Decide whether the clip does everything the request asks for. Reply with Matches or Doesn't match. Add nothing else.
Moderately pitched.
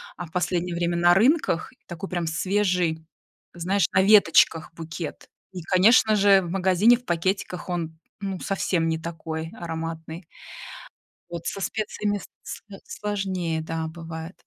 Matches